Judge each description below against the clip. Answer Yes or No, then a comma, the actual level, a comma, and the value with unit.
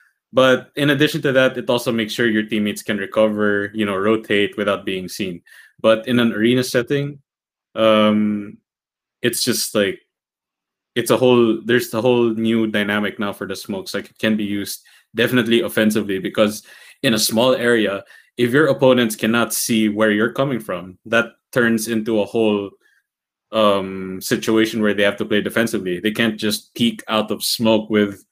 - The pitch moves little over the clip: Yes, narrow, 2.2 semitones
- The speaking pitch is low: Yes, low, 110 Hz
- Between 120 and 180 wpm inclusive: Yes, average, 175 wpm